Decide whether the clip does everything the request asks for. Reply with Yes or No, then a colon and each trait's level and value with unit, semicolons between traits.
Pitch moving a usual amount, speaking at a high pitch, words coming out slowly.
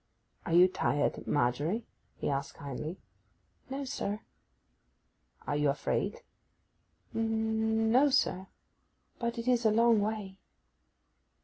No: wide, 6.2 semitones; high, 220 Hz; slow, 105 wpm